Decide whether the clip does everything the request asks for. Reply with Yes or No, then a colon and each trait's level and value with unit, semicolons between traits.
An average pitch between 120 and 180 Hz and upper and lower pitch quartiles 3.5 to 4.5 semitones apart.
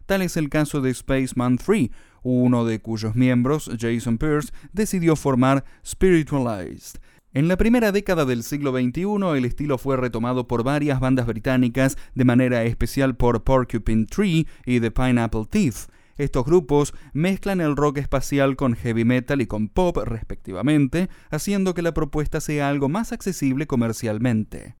Yes: low, 135 Hz; average, 4.1 semitones